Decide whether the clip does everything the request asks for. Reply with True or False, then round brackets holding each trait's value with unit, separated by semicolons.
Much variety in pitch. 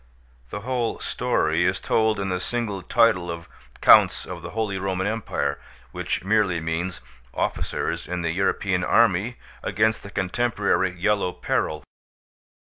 False (3.5 semitones)